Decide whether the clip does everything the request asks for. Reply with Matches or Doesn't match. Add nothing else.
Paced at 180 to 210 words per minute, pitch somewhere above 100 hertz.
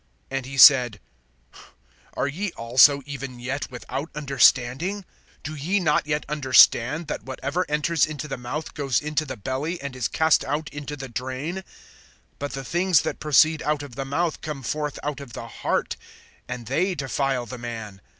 Doesn't match